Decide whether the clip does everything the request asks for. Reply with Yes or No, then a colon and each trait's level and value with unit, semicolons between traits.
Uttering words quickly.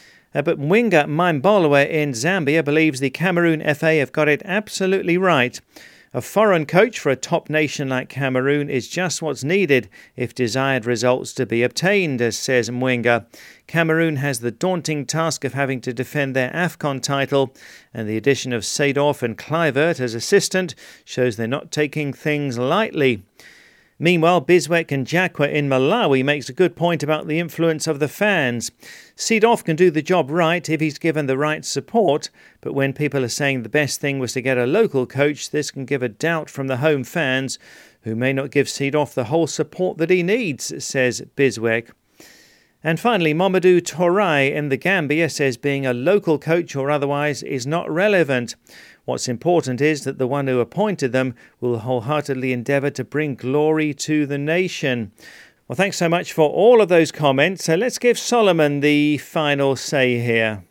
No: average, 175 wpm